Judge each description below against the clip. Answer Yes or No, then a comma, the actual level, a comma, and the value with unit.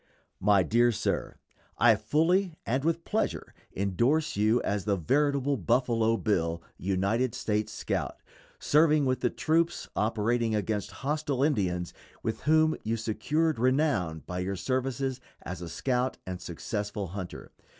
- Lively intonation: Yes, wide, 5.8 semitones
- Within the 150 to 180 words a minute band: No, average, 140 wpm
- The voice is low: Yes, low, 115 Hz